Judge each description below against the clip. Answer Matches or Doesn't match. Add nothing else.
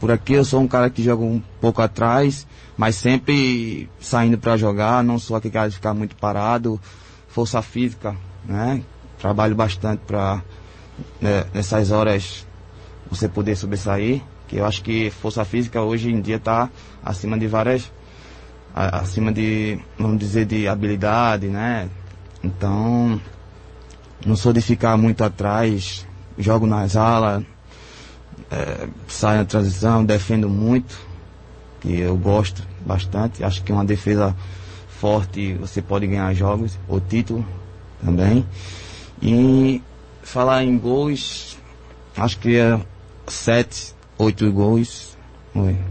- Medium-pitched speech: Doesn't match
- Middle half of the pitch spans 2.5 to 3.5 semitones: Matches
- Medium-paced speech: Matches